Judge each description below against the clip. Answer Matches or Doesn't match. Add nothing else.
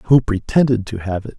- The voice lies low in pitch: Matches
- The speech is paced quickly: Matches